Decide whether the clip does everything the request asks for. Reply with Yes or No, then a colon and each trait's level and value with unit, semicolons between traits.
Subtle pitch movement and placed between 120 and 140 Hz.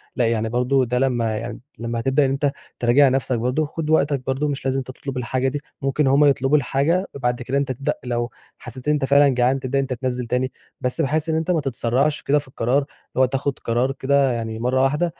Yes: narrow, 2.3 semitones; low, 135 Hz